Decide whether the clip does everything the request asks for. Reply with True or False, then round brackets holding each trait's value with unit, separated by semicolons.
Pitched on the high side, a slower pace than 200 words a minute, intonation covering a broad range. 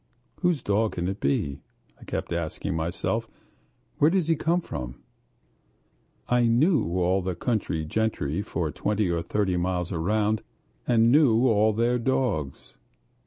False (105 Hz; 140 wpm; 5.9 semitones)